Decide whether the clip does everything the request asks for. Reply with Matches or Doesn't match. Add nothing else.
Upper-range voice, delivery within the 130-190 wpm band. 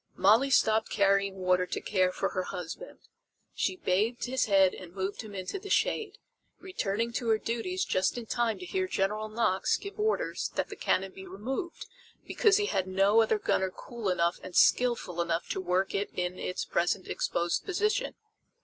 Matches